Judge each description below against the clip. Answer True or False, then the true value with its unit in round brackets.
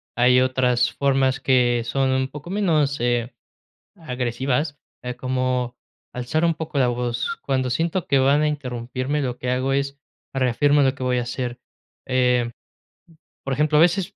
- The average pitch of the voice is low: True (130 Hz)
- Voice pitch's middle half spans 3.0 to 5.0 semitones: False (2.5 semitones)